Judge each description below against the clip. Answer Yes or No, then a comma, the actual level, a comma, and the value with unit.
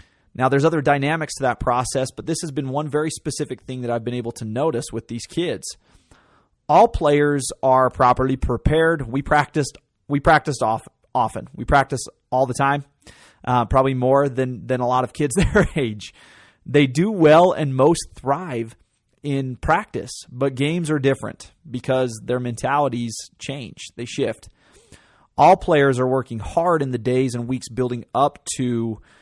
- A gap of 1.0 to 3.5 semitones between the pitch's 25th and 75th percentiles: Yes, average, 3.2 semitones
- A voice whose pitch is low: Yes, low, 130 Hz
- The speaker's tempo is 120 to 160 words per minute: No, average, 170 wpm